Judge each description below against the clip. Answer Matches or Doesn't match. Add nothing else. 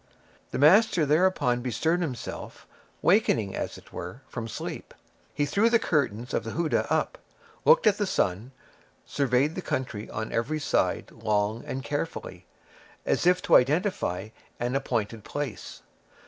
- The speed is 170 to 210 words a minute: Doesn't match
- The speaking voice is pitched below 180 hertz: Matches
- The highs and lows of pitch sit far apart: Matches